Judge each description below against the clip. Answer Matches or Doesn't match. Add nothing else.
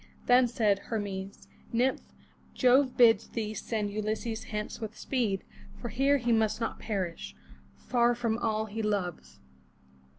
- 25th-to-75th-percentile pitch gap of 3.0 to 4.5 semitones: Doesn't match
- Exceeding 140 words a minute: Doesn't match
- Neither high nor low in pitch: Doesn't match